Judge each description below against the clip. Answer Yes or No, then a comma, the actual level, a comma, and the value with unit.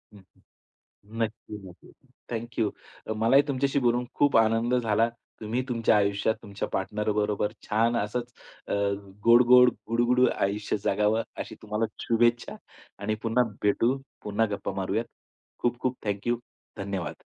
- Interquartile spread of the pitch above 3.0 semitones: No, narrow, 2.5 semitones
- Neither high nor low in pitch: No, low, 115 Hz